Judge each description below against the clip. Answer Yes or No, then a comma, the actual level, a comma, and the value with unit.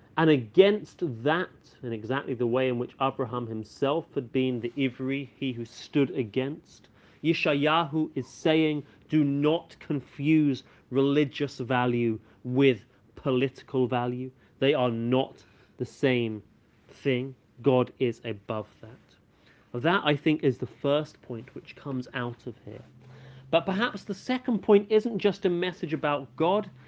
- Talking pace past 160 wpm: No, average, 145 wpm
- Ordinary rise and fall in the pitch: Yes, average, 3.9 semitones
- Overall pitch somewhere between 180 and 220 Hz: No, low, 130 Hz